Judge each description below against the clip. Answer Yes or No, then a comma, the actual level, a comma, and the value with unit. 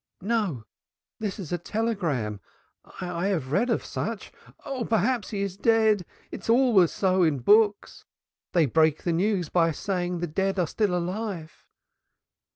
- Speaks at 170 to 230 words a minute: No, average, 155 wpm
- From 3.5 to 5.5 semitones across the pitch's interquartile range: Yes, average, 4.4 semitones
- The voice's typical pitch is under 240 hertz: Yes, medium, 185 Hz